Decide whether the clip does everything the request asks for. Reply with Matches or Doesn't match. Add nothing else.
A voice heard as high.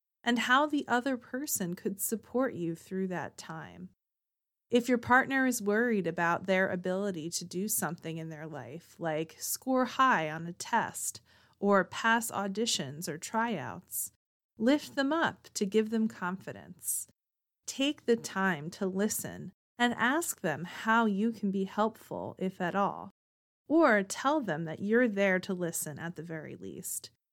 Matches